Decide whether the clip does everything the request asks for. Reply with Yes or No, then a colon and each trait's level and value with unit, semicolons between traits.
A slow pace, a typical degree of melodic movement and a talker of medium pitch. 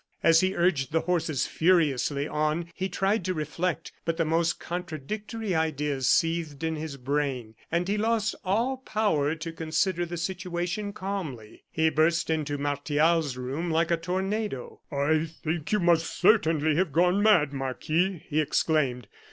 No: average, 150 wpm; average, 3.4 semitones; medium, 165 Hz